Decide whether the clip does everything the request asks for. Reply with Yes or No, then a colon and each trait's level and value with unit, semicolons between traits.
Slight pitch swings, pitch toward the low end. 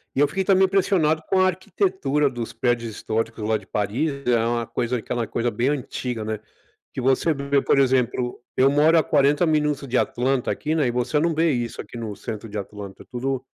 No: average, 4.2 semitones; low, 130 Hz